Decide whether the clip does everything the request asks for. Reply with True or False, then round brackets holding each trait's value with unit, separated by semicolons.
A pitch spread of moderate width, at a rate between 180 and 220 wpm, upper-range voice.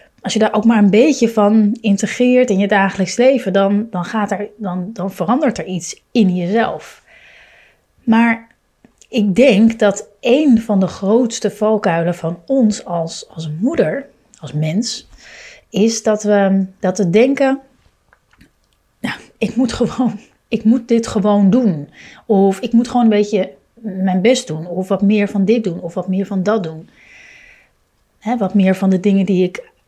False (3.3 semitones; 170 wpm; 210 Hz)